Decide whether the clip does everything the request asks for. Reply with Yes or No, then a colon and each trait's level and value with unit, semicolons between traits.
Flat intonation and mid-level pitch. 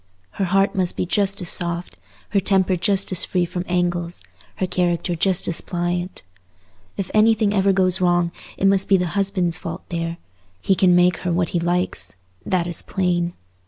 Yes: narrow, 1.8 semitones; medium, 180 Hz